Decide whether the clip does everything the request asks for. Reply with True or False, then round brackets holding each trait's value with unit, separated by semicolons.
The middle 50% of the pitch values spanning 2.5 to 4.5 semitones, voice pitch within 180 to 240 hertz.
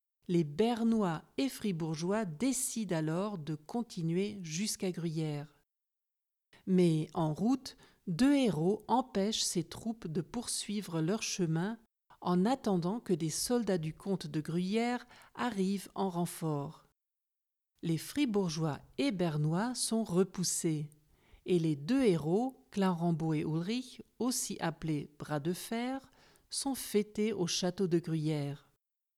False (5.4 semitones; 185 Hz)